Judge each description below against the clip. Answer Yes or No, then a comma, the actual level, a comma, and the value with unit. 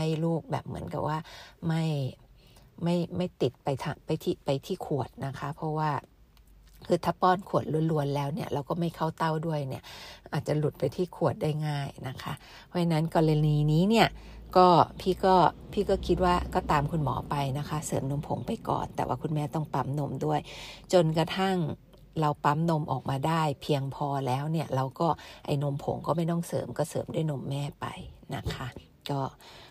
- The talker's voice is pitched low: No, medium, 150 Hz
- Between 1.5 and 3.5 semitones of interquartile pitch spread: Yes, average, 3.1 semitones